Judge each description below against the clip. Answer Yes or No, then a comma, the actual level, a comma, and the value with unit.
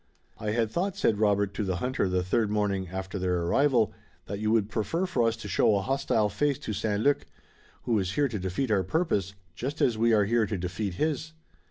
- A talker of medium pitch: No, low, 105 Hz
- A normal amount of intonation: Yes, average, 4.1 semitones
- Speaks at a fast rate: Yes, fast, 220 wpm